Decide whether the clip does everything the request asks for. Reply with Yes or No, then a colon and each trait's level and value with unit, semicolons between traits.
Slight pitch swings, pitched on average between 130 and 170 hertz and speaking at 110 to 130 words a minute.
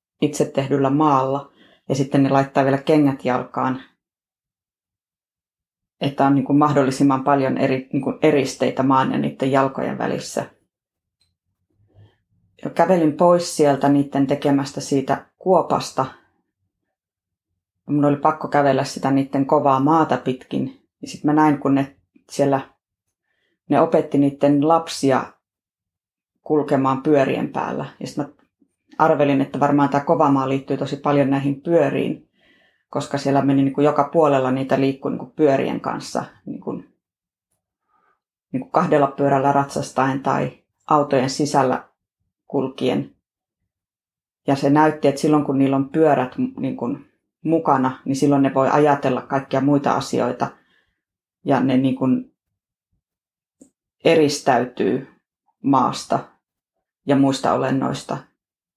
Yes: narrow, 1.6 semitones; medium, 140 Hz; average, 120 wpm